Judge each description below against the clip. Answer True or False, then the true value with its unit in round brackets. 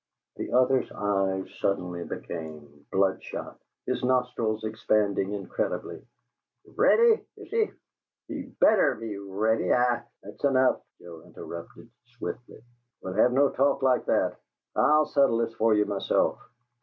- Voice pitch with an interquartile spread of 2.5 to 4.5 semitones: False (4.9 semitones)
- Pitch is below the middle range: True (110 Hz)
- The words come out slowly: True (130 wpm)